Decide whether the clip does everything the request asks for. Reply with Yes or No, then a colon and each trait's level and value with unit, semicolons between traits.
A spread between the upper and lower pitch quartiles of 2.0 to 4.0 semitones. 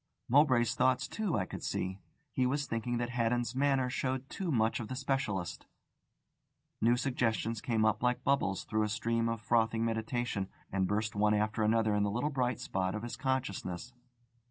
Yes: average, 3.0 semitones